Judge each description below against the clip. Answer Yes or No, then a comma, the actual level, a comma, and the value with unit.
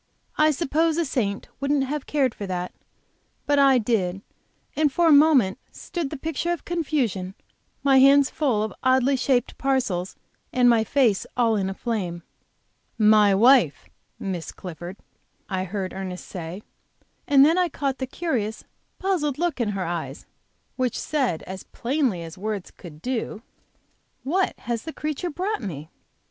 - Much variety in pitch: Yes, wide, 6.9 semitones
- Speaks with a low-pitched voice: No, very high, 250 Hz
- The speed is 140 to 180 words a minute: Yes, average, 155 wpm